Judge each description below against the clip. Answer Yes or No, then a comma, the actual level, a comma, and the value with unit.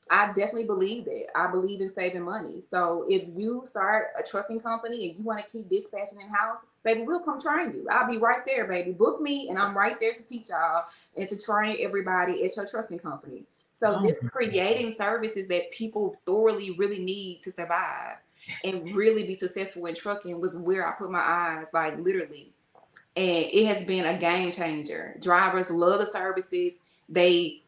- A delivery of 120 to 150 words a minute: No, average, 190 wpm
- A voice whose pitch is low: No, high, 195 Hz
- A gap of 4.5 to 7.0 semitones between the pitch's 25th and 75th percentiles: No, average, 3.8 semitones